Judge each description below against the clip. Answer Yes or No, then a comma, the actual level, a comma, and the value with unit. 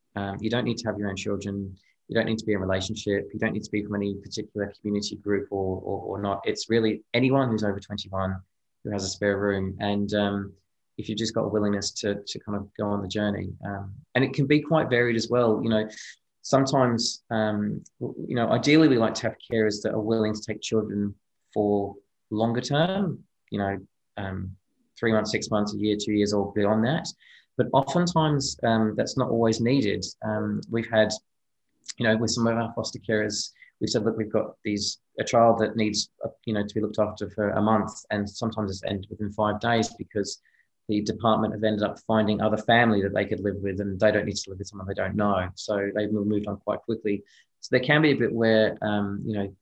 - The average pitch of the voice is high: No, low, 105 Hz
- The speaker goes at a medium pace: No, fast, 225 wpm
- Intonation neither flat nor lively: No, narrow, 1.9 semitones